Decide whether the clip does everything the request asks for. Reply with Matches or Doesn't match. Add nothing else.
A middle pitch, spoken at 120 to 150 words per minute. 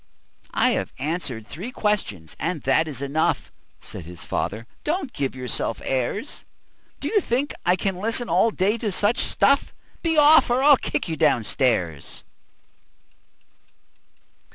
Matches